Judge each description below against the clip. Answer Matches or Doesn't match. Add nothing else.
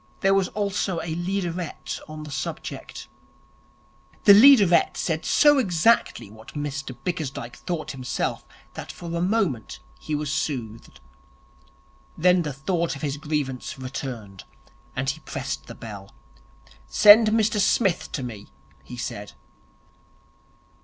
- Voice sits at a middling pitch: Matches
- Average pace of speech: Doesn't match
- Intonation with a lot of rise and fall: Matches